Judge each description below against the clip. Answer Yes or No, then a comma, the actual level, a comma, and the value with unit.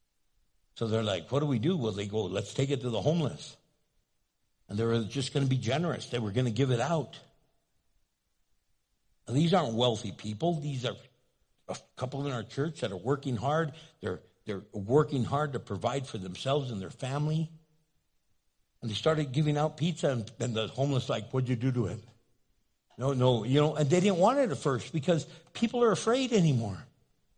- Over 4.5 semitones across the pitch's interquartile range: Yes, average, 5.0 semitones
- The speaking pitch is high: No, low, 135 Hz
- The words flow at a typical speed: Yes, average, 195 wpm